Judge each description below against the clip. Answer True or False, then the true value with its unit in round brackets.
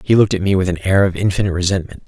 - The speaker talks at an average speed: False (290 wpm)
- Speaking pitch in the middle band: False (95 Hz)